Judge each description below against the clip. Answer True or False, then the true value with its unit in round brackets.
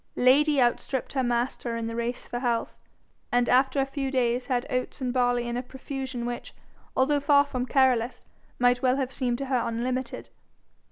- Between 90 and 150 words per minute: False (180 wpm)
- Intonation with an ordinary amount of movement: False (1.7 semitones)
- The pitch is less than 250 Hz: False (255 Hz)